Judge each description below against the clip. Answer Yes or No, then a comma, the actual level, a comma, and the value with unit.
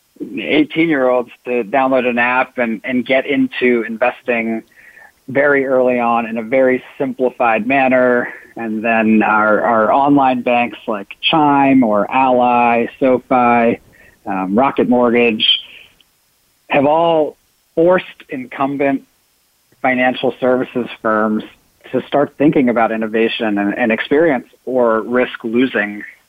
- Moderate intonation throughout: No, narrow, 2.2 semitones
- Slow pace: Yes, slow, 115 wpm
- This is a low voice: Yes, low, 125 Hz